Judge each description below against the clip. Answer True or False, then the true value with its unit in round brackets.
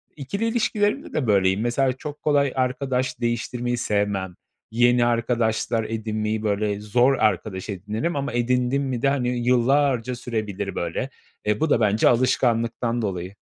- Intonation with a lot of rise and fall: False (3.4 semitones)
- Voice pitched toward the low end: True (120 Hz)